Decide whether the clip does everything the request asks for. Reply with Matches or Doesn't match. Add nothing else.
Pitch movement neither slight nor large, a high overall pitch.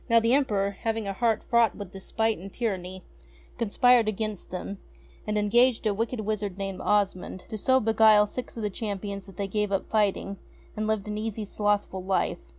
Doesn't match